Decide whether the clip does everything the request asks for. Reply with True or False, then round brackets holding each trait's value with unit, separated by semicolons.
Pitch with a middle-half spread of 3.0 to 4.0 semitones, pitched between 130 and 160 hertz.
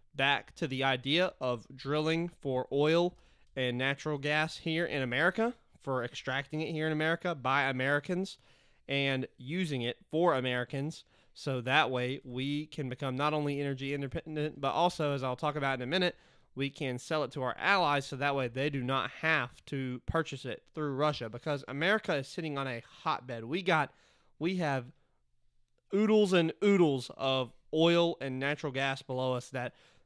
True (3.3 semitones; 140 Hz)